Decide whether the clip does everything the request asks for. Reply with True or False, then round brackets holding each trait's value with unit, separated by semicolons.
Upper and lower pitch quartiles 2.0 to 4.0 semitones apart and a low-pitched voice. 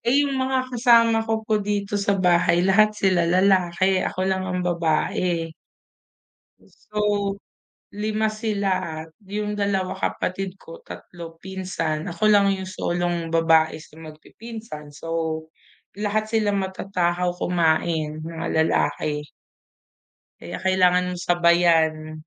False (3.7 semitones; 185 Hz)